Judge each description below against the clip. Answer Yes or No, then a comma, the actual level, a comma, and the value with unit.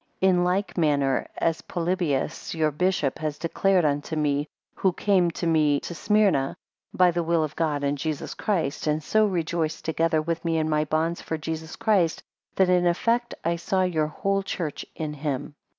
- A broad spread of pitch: No, average, 2.9 semitones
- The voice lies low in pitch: No, medium, 165 Hz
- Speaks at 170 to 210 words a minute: Yes, average, 180 wpm